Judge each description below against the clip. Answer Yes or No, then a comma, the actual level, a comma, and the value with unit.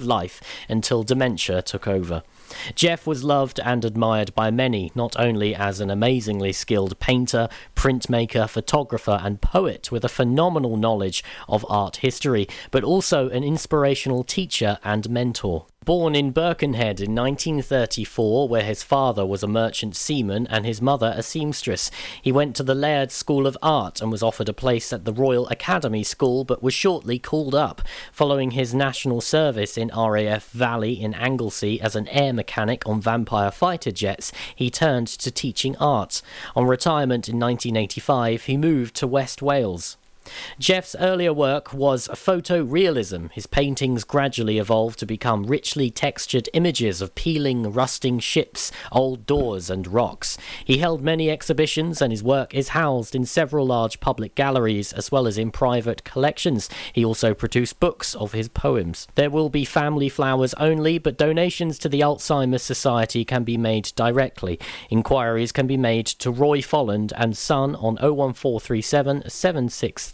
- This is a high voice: No, low, 125 Hz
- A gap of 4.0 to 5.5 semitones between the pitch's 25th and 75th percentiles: Yes, average, 4.3 semitones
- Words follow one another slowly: No, average, 155 wpm